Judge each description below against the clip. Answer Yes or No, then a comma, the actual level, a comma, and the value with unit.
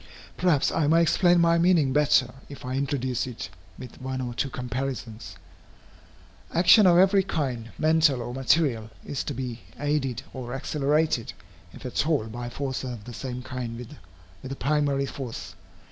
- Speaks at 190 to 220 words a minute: No, average, 160 wpm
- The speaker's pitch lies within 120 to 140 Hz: Yes, low, 135 Hz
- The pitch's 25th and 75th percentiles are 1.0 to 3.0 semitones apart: No, average, 3.6 semitones